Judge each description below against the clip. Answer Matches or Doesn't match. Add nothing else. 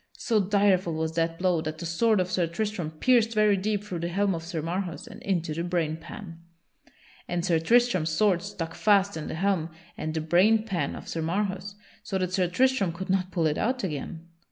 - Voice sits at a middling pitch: Matches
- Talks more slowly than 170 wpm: Doesn't match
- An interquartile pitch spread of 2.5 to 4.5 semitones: Matches